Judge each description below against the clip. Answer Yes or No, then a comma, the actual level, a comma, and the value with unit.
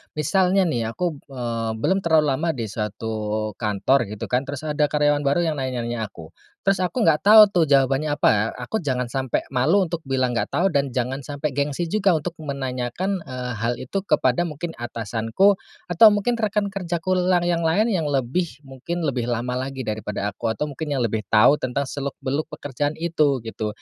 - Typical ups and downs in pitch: No, wide, 5.8 semitones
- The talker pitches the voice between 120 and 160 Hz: Yes, medium, 140 Hz